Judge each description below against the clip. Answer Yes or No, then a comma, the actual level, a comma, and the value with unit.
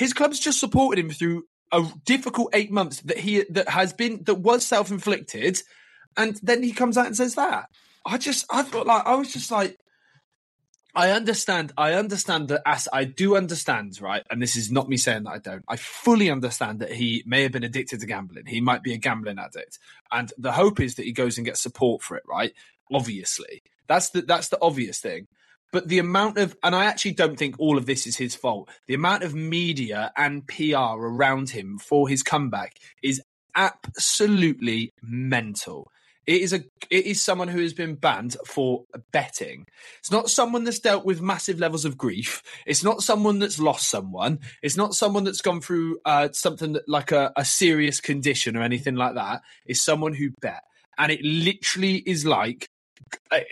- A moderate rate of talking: Yes, average, 195 wpm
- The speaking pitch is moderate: Yes, medium, 165 Hz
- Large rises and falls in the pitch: Yes, wide, 7.1 semitones